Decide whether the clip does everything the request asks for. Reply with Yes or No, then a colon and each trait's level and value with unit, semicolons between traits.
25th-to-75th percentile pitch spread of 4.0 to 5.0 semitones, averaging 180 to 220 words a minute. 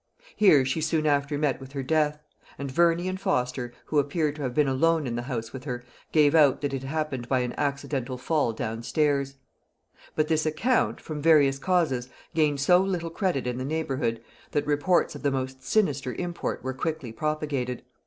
No: average, 3.2 semitones; average, 190 wpm